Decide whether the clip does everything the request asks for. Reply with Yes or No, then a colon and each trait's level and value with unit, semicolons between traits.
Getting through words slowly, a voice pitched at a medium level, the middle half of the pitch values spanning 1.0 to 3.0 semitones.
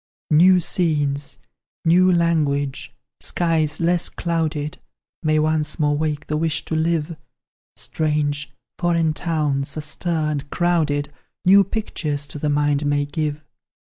Yes: slow, 120 wpm; medium, 155 Hz; narrow, 2.4 semitones